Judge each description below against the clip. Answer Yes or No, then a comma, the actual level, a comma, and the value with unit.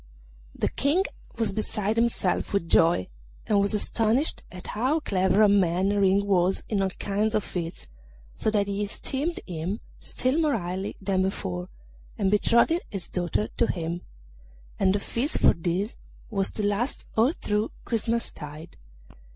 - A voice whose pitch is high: Yes, high, 200 Hz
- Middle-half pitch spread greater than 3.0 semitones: Yes, average, 3.4 semitones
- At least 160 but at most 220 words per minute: No, average, 150 wpm